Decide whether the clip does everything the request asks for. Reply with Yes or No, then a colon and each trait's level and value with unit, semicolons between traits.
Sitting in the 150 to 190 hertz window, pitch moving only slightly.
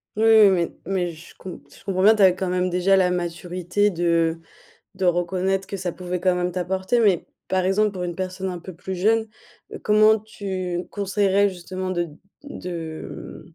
Yes: medium, 185 Hz; narrow, 1.7 semitones